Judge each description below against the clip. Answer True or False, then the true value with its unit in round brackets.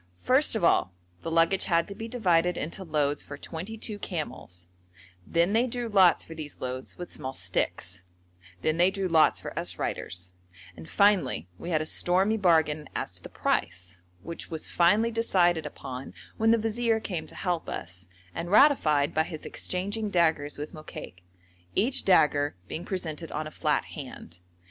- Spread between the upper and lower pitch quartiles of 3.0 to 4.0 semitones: False (5.1 semitones)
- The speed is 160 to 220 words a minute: True (170 wpm)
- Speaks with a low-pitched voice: False (170 Hz)